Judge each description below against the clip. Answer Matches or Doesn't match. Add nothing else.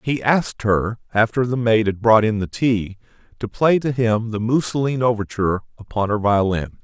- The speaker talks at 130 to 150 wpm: Doesn't match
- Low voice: Matches